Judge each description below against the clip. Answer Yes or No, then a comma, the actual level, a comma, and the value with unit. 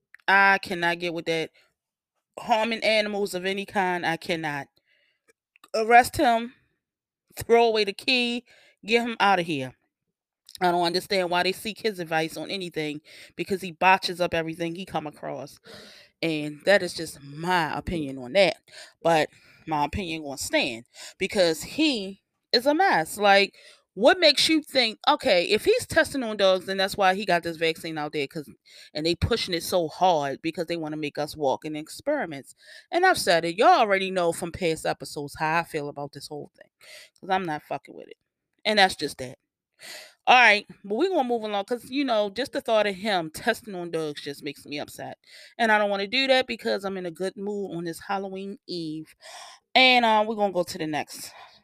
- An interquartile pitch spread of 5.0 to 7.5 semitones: Yes, wide, 5.5 semitones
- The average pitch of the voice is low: No, medium, 185 Hz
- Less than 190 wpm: No, average, 200 wpm